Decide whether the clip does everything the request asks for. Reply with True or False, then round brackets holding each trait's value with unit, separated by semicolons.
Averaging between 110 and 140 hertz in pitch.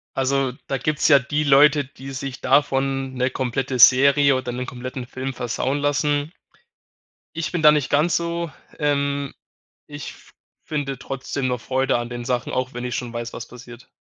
True (135 Hz)